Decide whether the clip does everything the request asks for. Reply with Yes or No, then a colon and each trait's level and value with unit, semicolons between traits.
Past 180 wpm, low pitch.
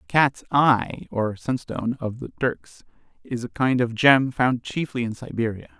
No: average, 175 wpm; low, 120 Hz